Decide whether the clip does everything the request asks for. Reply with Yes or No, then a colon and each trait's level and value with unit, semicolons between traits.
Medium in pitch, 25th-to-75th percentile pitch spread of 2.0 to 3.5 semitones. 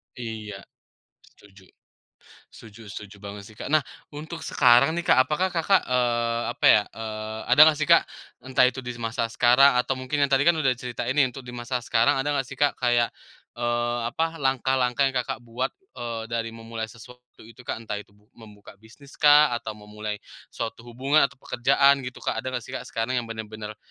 No: low, 120 Hz; average, 3.0 semitones